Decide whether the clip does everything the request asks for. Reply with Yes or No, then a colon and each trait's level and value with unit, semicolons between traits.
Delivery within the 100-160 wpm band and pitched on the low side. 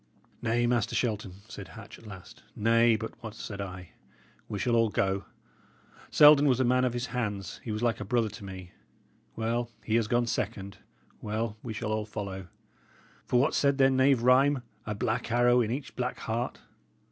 No: average, 185 wpm; low, 115 Hz